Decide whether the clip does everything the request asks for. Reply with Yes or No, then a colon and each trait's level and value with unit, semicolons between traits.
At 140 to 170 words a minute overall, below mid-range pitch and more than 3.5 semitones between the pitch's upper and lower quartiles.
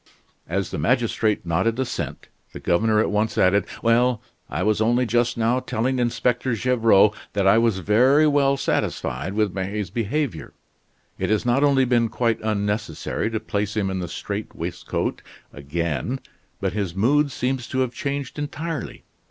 Yes: average, 160 wpm; low, 110 Hz; average, 4.1 semitones